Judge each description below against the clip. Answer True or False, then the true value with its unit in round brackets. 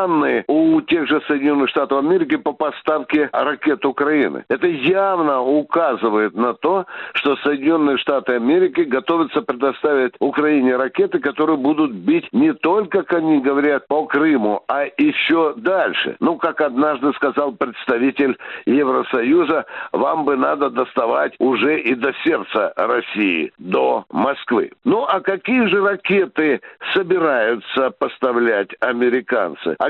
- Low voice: False (155 Hz)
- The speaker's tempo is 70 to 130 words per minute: True (125 wpm)